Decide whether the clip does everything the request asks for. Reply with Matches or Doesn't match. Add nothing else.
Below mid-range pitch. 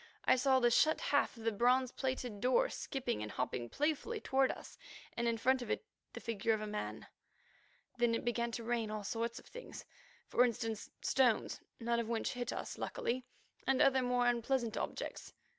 Doesn't match